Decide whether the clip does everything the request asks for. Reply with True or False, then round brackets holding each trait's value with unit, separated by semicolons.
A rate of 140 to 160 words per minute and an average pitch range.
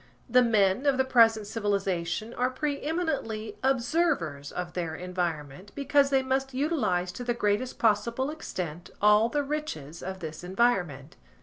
False (145 wpm; 6.8 semitones)